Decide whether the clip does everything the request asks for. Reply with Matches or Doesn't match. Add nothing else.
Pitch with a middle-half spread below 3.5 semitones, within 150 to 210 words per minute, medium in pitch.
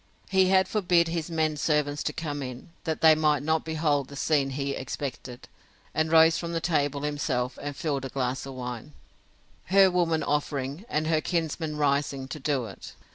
Matches